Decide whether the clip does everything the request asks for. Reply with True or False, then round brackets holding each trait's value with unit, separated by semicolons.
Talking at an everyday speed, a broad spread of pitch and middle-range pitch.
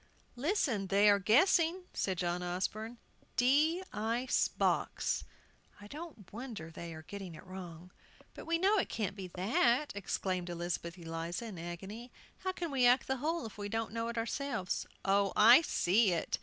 False (165 wpm; 6.0 semitones; 210 Hz)